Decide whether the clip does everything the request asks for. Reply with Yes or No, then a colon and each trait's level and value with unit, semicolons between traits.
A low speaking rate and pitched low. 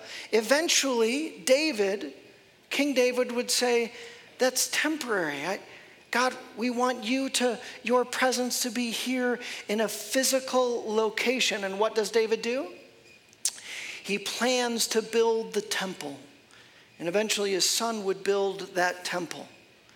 No: slow, 125 wpm; high, 235 Hz